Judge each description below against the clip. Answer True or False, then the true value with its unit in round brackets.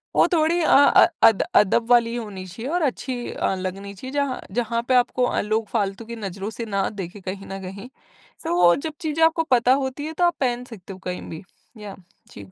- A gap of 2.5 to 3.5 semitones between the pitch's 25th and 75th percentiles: False (5.1 semitones)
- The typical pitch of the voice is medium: False (230 Hz)